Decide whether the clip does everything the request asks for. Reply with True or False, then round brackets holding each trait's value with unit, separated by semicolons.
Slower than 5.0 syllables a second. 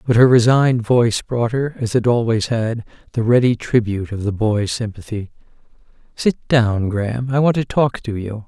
False (5.2 syllables/s)